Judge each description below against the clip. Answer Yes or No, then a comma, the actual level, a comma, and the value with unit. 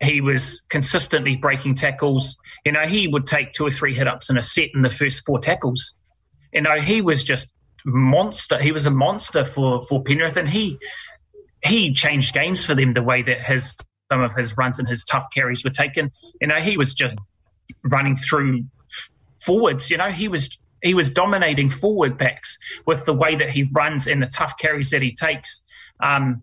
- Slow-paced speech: No, average, 200 wpm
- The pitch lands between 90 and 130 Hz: No, medium, 140 Hz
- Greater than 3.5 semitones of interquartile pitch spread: No, average, 3.1 semitones